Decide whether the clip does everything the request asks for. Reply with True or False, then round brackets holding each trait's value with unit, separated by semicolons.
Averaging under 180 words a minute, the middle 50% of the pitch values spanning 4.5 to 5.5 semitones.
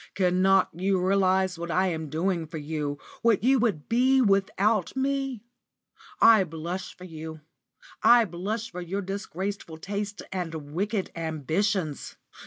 False (135 wpm; 3.9 semitones)